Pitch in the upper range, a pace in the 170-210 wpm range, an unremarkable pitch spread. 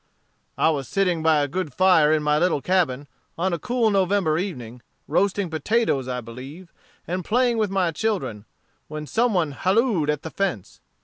No: medium, 170 Hz; average, 175 wpm; average, 4.8 semitones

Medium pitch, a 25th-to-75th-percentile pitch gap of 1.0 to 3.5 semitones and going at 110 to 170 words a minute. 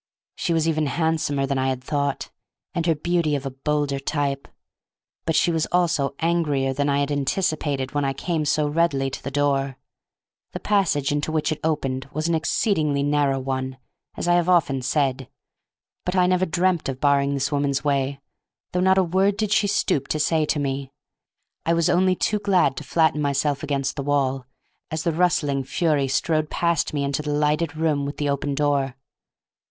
No: medium, 145 Hz; average, 3.2 semitones; average, 190 wpm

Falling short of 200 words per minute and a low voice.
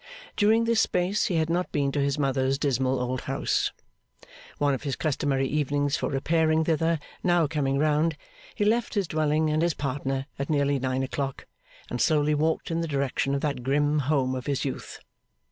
No: average, 185 wpm; medium, 145 Hz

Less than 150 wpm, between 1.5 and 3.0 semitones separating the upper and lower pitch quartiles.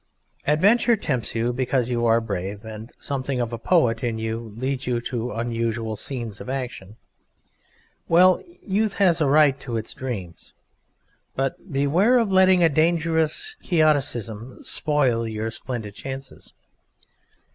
No: slow, 135 wpm; wide, 5.4 semitones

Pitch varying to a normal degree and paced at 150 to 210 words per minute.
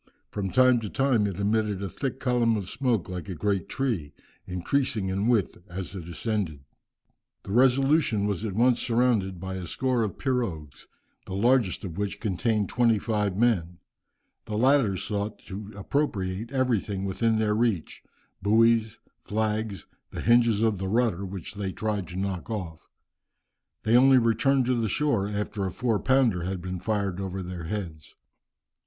Yes: average, 3.7 semitones; average, 160 wpm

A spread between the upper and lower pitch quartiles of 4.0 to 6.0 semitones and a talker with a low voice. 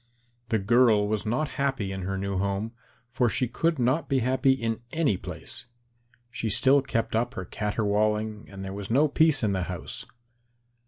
Yes: average, 4.6 semitones; low, 115 Hz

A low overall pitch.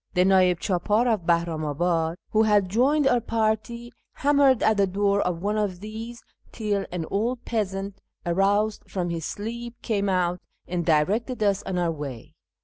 No: high, 200 Hz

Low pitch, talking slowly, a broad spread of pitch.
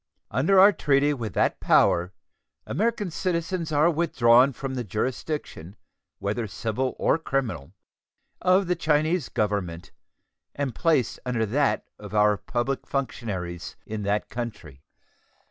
Yes: low, 130 Hz; slow, 125 wpm; wide, 6.8 semitones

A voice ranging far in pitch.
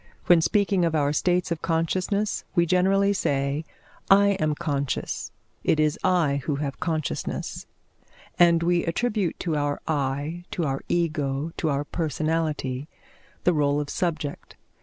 No: average, 3.4 semitones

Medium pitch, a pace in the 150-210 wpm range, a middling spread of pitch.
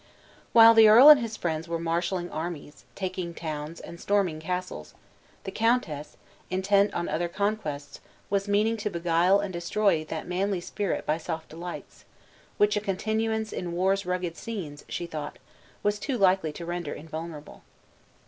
Yes: medium, 180 Hz; average, 155 wpm; average, 3.8 semitones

